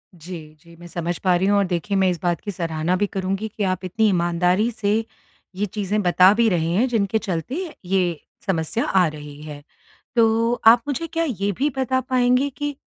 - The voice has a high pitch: Yes, high, 195 Hz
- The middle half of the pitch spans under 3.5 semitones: No, average, 4.6 semitones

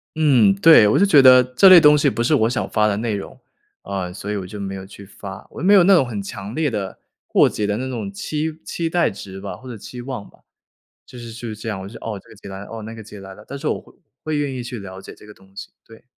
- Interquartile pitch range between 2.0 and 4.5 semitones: No, wide, 5.4 semitones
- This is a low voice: Yes, low, 110 Hz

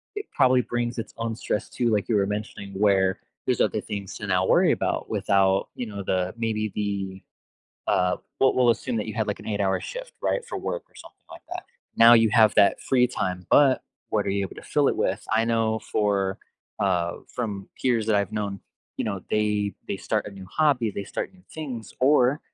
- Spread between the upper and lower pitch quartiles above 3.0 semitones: Yes, average, 3.4 semitones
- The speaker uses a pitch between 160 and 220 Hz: No, low, 105 Hz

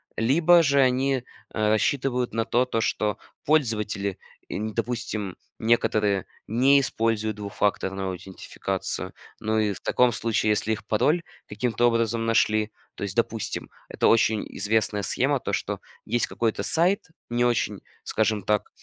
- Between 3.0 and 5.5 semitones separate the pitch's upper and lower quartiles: No, narrow, 2.5 semitones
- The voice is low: Yes, low, 115 Hz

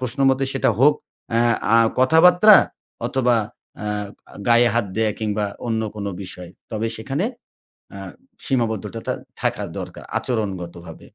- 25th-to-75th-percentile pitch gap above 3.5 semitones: Yes, average, 4.0 semitones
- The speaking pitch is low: Yes, low, 115 Hz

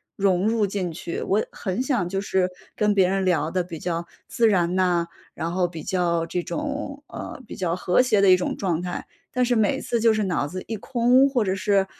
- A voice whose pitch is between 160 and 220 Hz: Yes, high, 190 Hz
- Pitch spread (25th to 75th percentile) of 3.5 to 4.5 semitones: Yes, average, 3.8 semitones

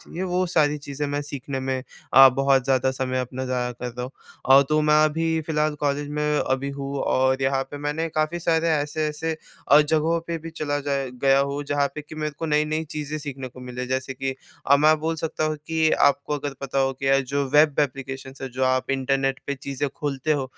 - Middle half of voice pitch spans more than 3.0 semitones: No, narrow, 2.4 semitones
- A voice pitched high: No, medium, 140 Hz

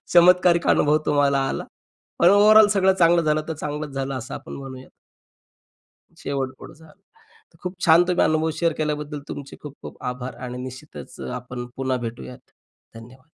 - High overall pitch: No, medium, 150 Hz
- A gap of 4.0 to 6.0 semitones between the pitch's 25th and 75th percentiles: Yes, average, 4.4 semitones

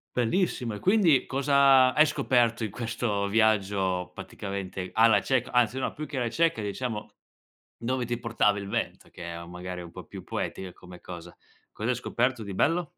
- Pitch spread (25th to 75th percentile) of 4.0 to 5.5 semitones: Yes, average, 4.8 semitones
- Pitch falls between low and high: No, low, 115 Hz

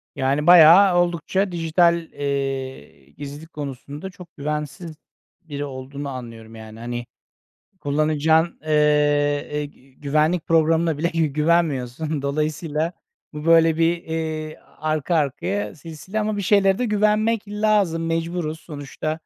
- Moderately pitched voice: Yes, medium, 155 Hz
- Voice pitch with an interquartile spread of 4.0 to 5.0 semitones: No, average, 3.0 semitones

